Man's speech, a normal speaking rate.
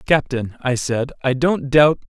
Yes: male; average, 170 wpm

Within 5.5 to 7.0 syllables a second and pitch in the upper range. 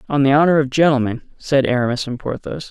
No: 6.0 syllables/s; low, 135 Hz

